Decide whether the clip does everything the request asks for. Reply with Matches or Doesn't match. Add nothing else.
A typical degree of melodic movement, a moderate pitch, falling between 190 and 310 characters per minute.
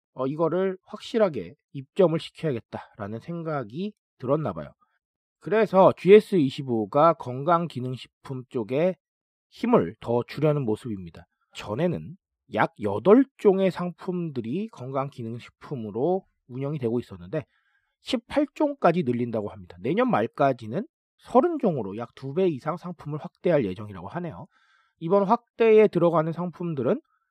Doesn't match